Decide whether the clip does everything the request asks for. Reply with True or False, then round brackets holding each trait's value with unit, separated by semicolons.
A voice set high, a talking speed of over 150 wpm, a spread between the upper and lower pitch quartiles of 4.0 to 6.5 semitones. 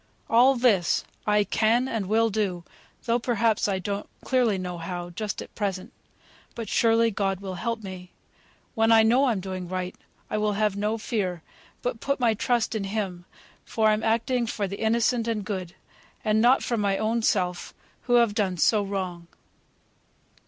False (215 Hz; 175 wpm; 3.2 semitones)